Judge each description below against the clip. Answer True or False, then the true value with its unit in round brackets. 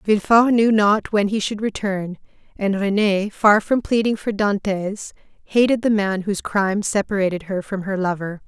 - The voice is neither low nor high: False (205 Hz)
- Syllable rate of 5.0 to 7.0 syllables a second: False (4.7 syllables/s)